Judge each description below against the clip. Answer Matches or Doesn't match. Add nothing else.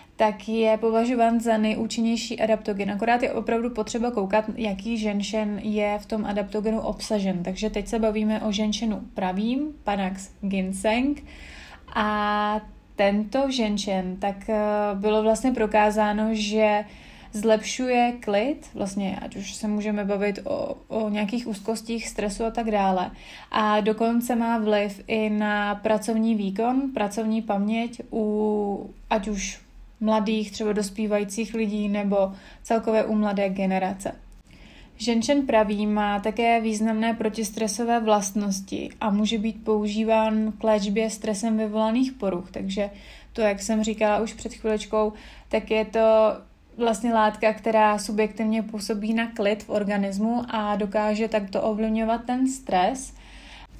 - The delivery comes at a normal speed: Matches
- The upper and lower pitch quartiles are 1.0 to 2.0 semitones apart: Matches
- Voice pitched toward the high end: Matches